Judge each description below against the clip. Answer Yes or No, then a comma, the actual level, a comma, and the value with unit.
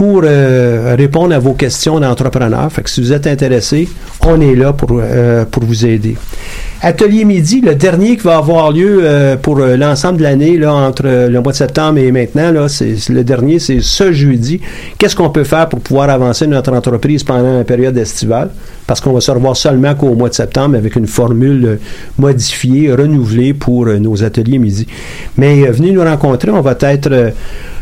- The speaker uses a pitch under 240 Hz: Yes, low, 135 Hz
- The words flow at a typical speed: Yes, average, 195 wpm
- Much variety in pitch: No, average, 3.8 semitones